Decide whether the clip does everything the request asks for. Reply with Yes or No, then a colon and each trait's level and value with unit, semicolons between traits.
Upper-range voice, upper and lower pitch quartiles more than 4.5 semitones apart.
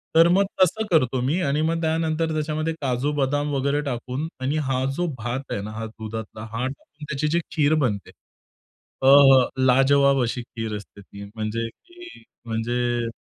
No: low, 135 Hz; average, 4.9 semitones